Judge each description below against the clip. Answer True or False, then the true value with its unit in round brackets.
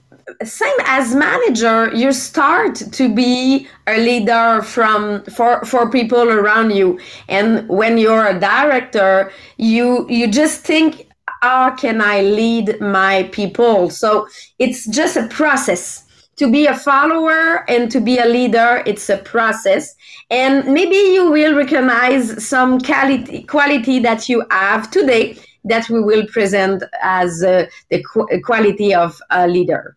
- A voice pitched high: True (235 Hz)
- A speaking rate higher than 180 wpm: False (140 wpm)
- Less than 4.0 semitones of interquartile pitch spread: False (4.3 semitones)